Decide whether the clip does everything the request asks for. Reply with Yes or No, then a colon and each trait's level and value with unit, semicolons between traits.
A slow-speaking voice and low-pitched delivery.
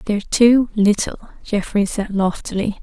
No: slow, 125 wpm; high, 210 Hz